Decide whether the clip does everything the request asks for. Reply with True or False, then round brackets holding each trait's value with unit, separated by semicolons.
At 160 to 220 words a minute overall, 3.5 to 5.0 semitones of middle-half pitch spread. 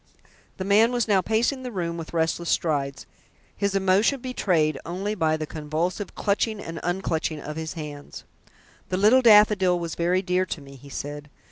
True (170 wpm; 4.5 semitones)